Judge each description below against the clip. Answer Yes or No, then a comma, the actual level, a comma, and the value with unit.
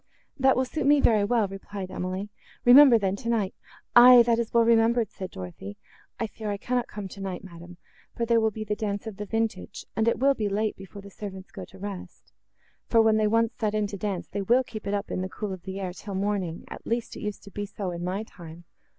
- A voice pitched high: Yes, high, 210 Hz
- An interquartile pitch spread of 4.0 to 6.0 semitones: No, average, 3.1 semitones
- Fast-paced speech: Yes, fast, 240 wpm